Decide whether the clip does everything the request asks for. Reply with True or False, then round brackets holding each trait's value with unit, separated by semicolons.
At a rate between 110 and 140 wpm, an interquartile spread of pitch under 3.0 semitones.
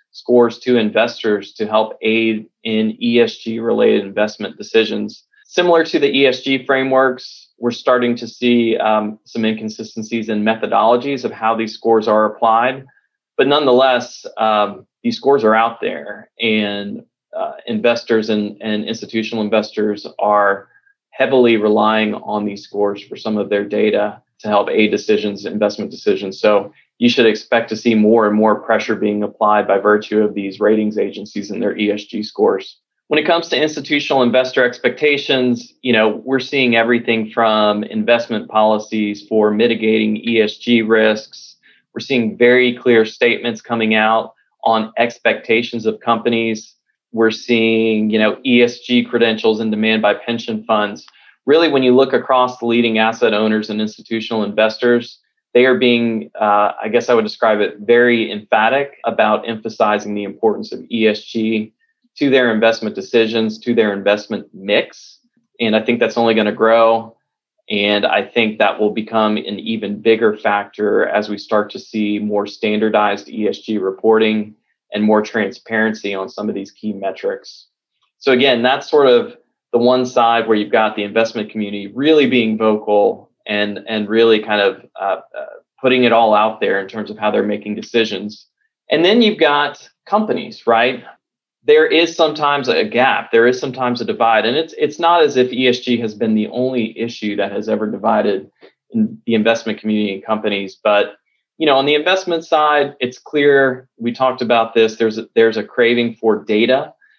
False (165 wpm; 2.6 semitones)